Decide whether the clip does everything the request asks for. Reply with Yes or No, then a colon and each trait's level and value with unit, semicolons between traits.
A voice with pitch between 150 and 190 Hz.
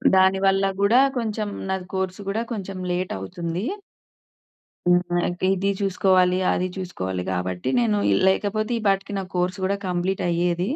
Yes: medium, 185 Hz